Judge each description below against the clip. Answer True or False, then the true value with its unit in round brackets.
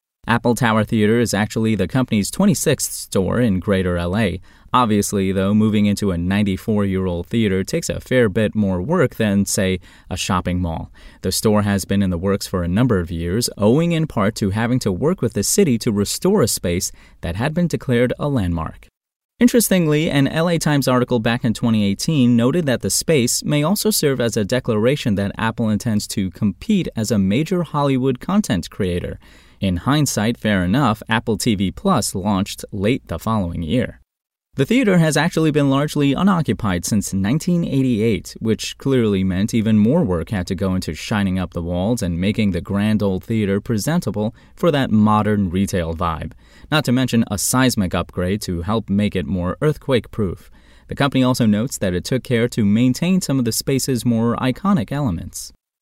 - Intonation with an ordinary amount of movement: True (4.9 semitones)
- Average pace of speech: True (180 wpm)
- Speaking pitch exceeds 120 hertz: False (110 Hz)